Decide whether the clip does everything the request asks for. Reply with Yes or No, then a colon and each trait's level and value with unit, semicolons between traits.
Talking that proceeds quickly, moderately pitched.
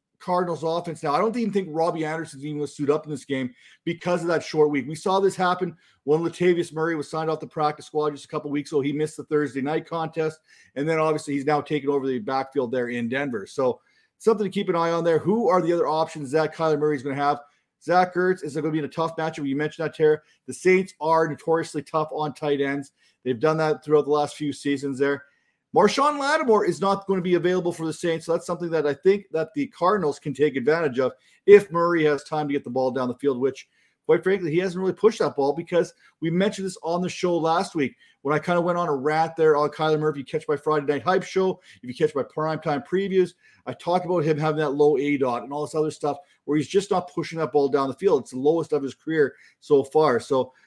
Yes: fast, 260 wpm; medium, 155 Hz